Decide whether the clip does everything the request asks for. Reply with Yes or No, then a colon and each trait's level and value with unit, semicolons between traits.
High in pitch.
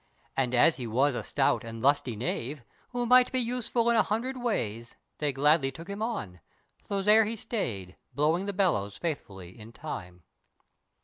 No: medium, 150 Hz